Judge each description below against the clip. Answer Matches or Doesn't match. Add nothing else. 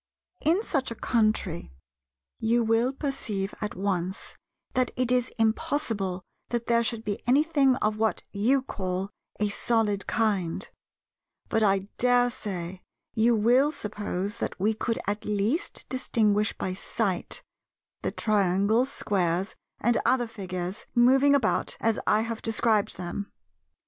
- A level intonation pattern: Doesn't match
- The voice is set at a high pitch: Matches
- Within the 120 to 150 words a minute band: Matches